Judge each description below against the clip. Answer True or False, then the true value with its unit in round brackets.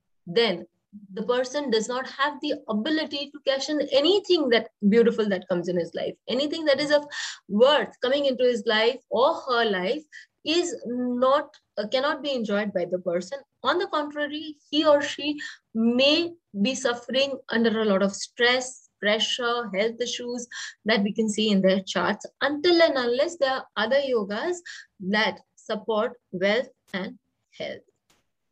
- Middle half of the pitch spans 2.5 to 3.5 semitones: False (5.1 semitones)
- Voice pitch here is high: True (245 Hz)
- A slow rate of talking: False (160 wpm)